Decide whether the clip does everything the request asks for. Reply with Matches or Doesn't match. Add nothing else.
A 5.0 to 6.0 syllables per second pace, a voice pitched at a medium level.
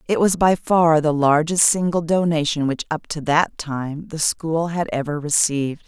Doesn't match